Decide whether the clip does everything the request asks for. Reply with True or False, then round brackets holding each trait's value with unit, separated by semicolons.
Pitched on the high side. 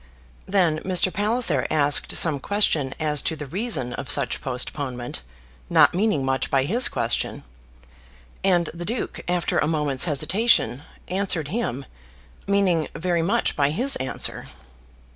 False (160 Hz)